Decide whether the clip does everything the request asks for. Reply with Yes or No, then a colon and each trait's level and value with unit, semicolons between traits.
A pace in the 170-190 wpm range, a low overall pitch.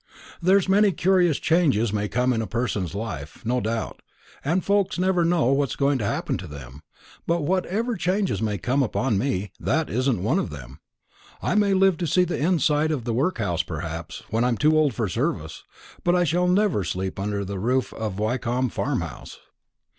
Yes: average, 185 wpm; low, 130 Hz